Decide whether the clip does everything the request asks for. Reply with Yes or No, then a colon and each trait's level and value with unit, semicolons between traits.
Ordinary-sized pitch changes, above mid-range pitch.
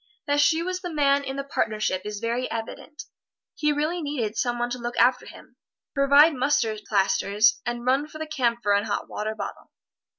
Yes: average, 5.0 semitones; very high, 250 Hz